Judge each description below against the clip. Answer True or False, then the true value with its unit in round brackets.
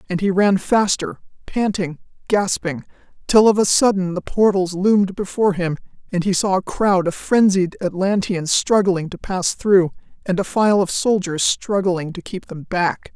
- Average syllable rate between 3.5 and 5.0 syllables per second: True (4.5 syllables/s)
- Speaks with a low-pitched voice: False (190 Hz)